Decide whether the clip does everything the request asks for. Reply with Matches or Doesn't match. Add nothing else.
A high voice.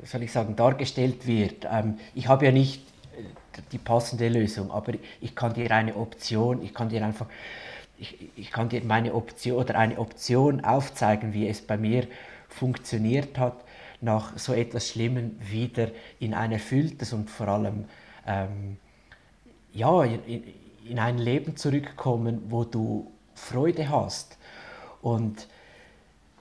Doesn't match